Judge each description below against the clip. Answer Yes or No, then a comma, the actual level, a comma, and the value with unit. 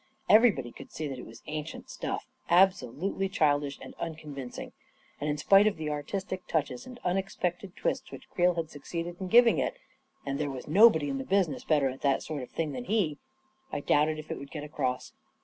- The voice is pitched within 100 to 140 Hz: No, medium, 155 Hz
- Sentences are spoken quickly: Yes, fast, 220 wpm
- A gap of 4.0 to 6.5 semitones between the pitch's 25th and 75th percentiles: Yes, average, 5.1 semitones